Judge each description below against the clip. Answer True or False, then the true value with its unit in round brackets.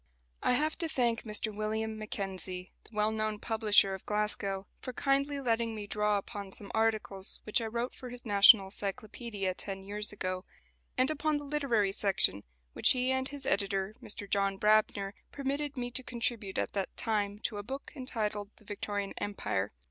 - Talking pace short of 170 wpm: False (175 wpm)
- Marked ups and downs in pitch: False (3.5 semitones)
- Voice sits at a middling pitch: False (215 Hz)